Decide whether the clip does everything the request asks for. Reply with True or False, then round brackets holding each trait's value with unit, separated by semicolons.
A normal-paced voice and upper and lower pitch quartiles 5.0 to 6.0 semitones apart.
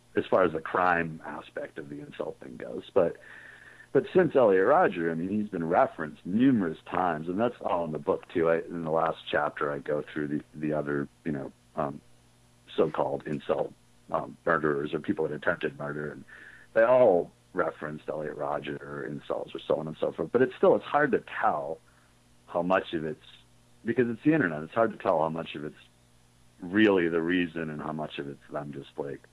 False (210 wpm; 5.4 semitones)